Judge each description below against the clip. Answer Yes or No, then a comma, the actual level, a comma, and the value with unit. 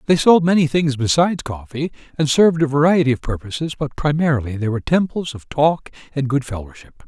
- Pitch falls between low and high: Yes, medium, 145 Hz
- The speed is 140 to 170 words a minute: No, average, 185 wpm